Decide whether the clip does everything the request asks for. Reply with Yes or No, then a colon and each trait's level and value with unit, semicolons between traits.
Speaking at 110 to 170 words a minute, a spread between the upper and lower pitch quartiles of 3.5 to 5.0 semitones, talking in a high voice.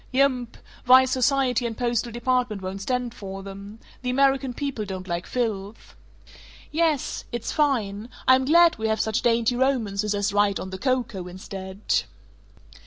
Yes: average, 150 wpm; average, 4.5 semitones; high, 235 Hz